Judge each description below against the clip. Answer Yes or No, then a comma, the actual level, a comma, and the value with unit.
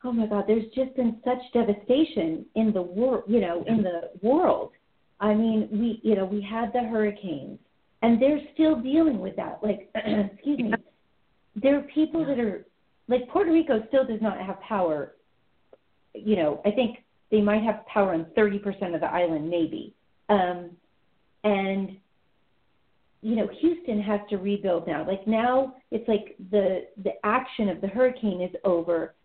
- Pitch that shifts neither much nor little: Yes, average, 4.0 semitones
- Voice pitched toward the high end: Yes, high, 215 Hz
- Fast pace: No, average, 170 wpm